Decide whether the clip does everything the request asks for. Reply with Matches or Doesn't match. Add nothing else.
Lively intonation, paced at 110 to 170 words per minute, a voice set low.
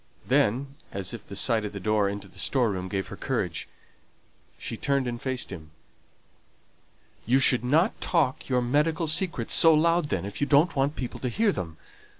Doesn't match